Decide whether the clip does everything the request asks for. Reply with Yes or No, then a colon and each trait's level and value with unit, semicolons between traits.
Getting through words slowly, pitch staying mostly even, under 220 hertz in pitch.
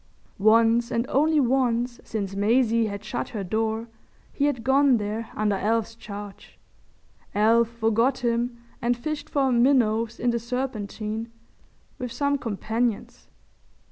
No: slow, 130 wpm; narrow, 2.3 semitones; high, 230 Hz